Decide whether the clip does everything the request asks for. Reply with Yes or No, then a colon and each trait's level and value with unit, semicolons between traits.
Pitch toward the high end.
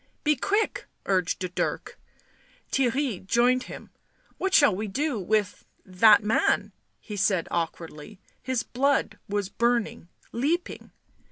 Yes: high, 225 Hz